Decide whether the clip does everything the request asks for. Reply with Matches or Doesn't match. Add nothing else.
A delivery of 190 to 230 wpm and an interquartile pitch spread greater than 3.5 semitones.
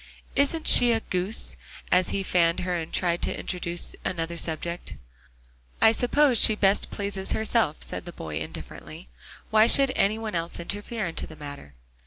Doesn't match